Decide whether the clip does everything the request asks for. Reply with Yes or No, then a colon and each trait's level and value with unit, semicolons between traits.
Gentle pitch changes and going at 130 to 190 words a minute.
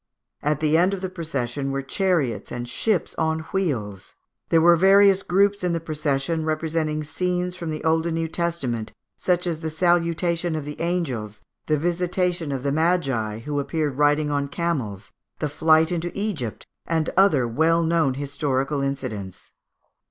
No: average, 3.8 semitones; average, 160 wpm